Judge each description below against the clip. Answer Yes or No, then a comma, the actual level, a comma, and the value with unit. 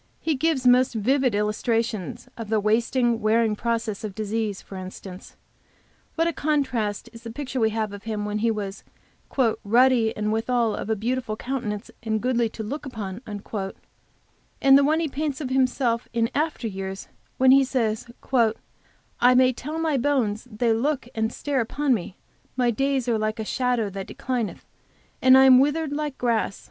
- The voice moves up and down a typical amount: Yes, average, 3.5 semitones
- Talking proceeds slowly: No, average, 175 wpm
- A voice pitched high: Yes, high, 235 Hz